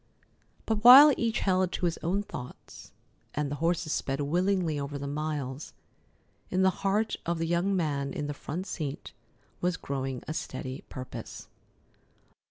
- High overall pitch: No, medium, 160 Hz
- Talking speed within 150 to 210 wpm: Yes, average, 155 wpm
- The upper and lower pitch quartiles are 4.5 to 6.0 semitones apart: Yes, average, 4.9 semitones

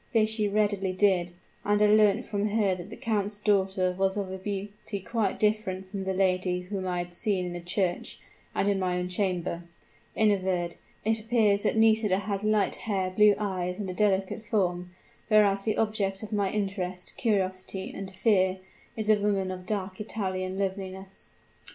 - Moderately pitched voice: No, high, 195 Hz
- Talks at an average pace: Yes, average, 180 wpm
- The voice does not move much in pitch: Yes, narrow, 2.1 semitones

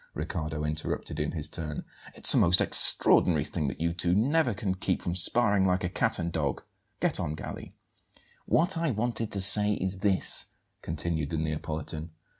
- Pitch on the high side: No, very low, 85 Hz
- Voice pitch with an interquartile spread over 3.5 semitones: Yes, average, 4.6 semitones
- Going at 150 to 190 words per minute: Yes, average, 175 wpm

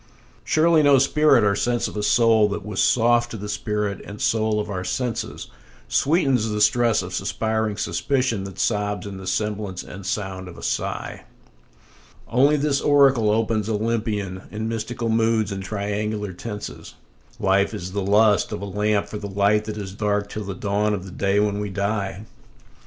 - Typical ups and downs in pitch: No, narrow, 2.2 semitones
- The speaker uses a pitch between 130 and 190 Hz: No, low, 105 Hz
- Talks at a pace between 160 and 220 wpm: Yes, average, 180 wpm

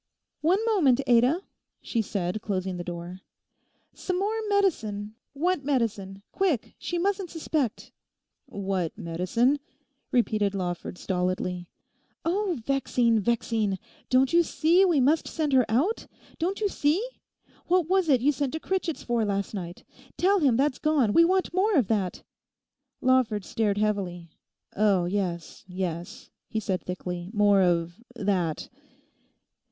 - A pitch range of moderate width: No, wide, 8.9 semitones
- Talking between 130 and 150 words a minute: Yes, slow, 135 wpm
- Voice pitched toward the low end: No, high, 230 Hz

